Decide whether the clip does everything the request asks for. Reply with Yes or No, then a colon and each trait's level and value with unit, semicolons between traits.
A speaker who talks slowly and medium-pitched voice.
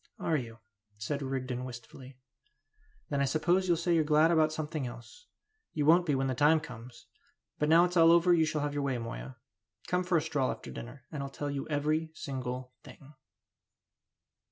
No: average, 190 wpm; medium, 145 Hz